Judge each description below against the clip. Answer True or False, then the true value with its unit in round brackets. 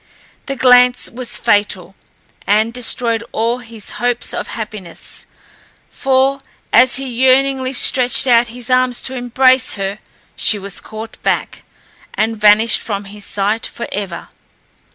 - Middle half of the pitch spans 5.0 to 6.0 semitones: False (3.1 semitones)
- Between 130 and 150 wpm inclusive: True (135 wpm)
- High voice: True (235 Hz)